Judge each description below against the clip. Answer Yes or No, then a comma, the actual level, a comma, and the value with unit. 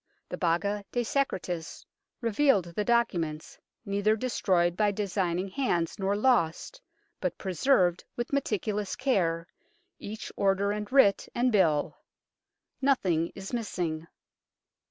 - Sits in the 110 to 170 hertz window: No, high, 200 Hz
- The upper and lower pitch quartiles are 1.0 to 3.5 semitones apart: No, average, 5.2 semitones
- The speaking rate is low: Yes, slow, 115 wpm